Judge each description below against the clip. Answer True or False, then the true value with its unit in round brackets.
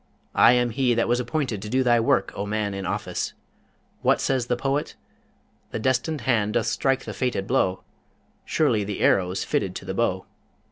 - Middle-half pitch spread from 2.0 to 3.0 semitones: False (3.7 semitones)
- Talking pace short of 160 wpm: False (185 wpm)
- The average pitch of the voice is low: True (120 Hz)